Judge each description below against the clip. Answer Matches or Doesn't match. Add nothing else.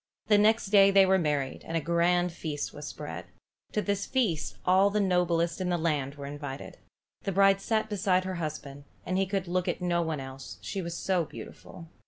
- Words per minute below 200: Doesn't match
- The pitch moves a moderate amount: Matches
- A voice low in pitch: Doesn't match